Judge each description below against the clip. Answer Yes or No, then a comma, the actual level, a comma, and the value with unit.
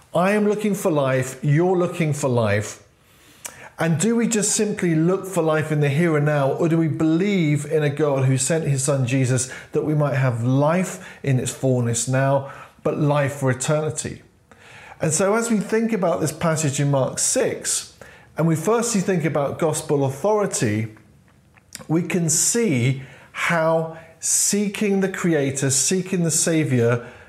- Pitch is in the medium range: Yes, medium, 155 Hz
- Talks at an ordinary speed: Yes, average, 165 wpm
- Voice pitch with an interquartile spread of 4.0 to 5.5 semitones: Yes, average, 4.8 semitones